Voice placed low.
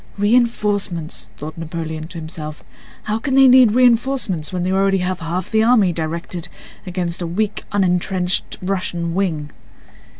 No: medium, 185 Hz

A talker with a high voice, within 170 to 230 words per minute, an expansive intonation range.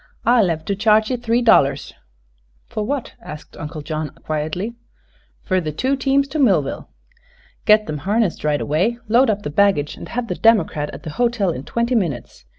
Yes: high, 200 Hz; average, 180 wpm; wide, 7.3 semitones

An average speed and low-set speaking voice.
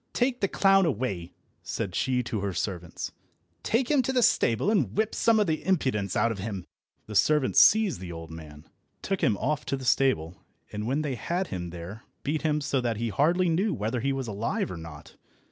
No: fast, 210 wpm; low, 125 Hz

